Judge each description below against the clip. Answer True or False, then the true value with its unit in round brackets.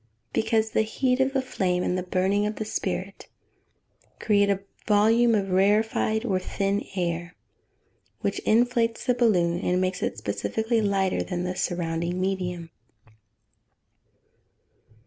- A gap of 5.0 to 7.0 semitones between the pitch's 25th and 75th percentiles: False (3.5 semitones)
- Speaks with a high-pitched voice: True (200 Hz)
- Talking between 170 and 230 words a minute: False (140 wpm)